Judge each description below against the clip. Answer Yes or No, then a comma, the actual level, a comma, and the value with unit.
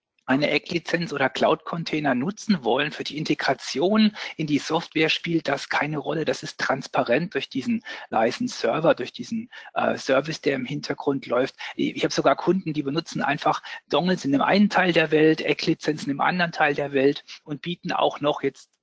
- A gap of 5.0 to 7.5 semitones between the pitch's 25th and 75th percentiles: No, average, 3.7 semitones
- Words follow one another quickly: No, average, 175 wpm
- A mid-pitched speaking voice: Yes, medium, 155 Hz